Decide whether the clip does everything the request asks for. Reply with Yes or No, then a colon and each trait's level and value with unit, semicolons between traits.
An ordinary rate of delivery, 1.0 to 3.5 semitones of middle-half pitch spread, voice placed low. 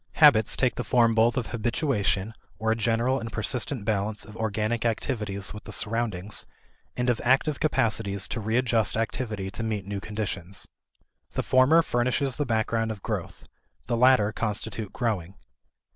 Yes: average, 155 wpm; average, 2.7 semitones; low, 110 Hz